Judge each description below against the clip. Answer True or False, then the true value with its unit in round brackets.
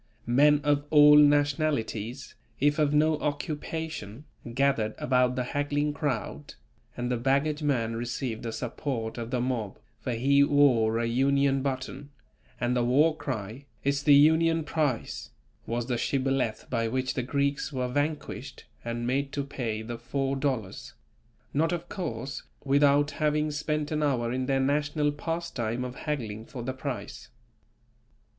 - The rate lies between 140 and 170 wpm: True (150 wpm)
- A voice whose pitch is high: False (135 Hz)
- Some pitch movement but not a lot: True (3.3 semitones)